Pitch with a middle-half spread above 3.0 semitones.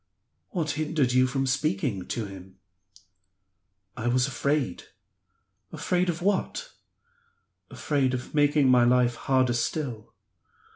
Yes: average, 3.8 semitones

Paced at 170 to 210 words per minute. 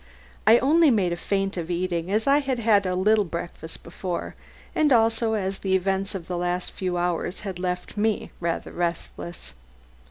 Yes: average, 180 wpm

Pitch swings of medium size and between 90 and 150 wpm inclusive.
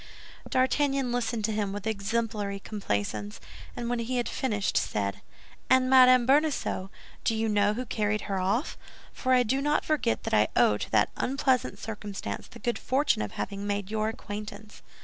No: average, 4.1 semitones; average, 170 wpm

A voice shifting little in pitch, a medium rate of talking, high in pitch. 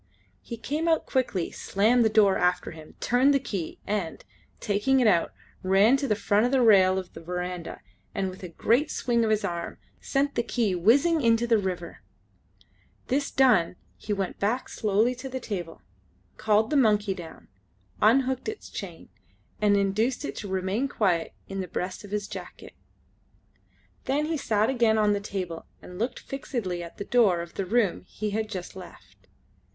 No: average, 4.7 semitones; average, 175 wpm; high, 210 Hz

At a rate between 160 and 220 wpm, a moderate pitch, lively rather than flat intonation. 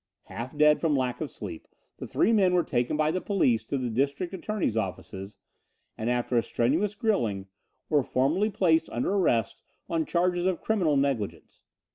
Yes: average, 170 wpm; medium, 150 Hz; wide, 7.1 semitones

